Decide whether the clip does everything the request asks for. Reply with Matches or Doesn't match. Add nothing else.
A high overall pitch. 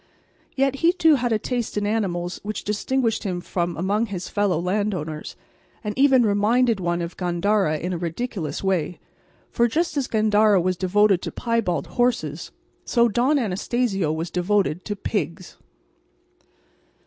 Matches